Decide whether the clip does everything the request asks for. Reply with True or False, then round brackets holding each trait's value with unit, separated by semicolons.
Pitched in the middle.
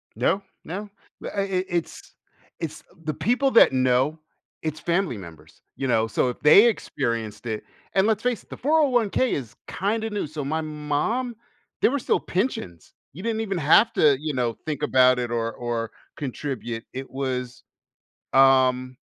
True (150 Hz)